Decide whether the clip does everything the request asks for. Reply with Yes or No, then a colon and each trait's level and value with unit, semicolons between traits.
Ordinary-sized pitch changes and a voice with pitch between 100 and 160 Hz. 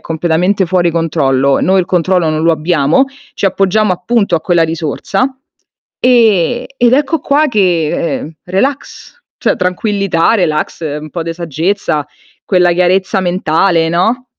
No: average, 3.7 semitones; medium, 180 Hz